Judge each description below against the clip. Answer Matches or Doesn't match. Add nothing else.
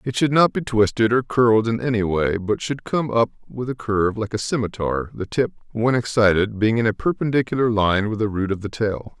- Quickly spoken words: Matches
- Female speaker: Doesn't match